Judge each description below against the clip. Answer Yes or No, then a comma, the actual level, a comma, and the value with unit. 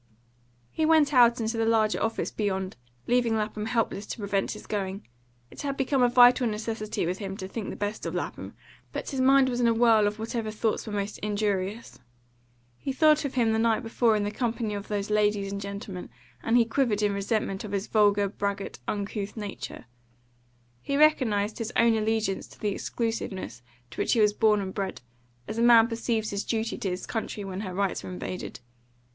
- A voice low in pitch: No, high, 215 Hz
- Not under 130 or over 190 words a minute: No, average, 200 wpm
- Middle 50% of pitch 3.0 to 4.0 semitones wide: No, narrow, 2.5 semitones